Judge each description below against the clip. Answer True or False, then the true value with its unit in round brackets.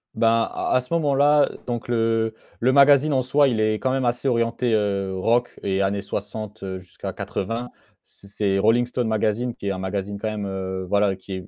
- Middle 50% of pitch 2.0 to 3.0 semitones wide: False (3.8 semitones)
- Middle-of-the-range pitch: False (110 Hz)